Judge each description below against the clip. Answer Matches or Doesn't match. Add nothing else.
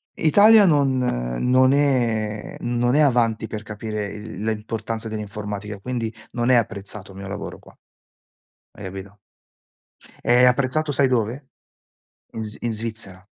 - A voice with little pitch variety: Doesn't match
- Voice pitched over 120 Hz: Doesn't match